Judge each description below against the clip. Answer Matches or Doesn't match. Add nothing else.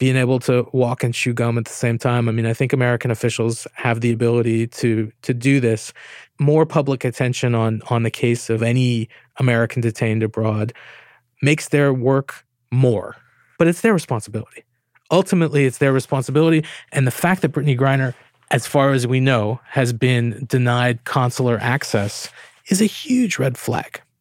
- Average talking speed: Matches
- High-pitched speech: Doesn't match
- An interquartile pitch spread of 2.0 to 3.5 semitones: Matches